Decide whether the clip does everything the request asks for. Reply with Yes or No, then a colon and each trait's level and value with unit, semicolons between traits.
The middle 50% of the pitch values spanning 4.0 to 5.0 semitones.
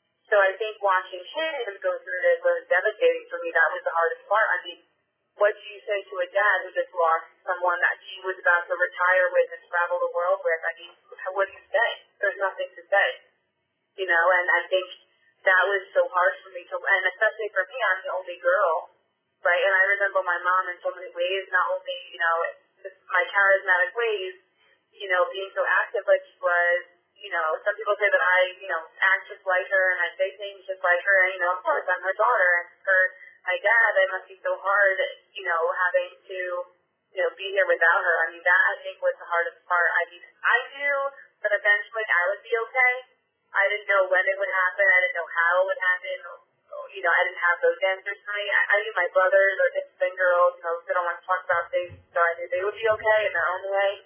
No: narrow, 2.6 semitones